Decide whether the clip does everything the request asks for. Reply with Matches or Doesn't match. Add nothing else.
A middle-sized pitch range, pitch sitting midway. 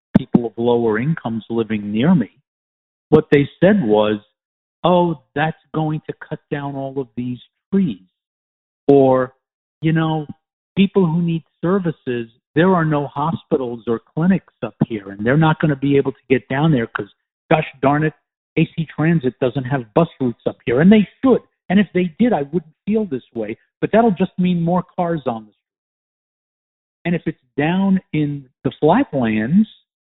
Doesn't match